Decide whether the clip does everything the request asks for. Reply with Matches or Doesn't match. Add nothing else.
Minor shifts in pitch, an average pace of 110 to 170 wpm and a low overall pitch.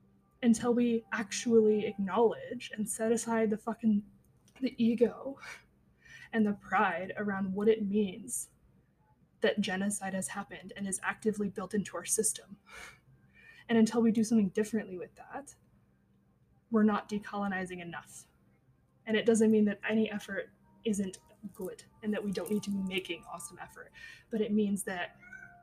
Doesn't match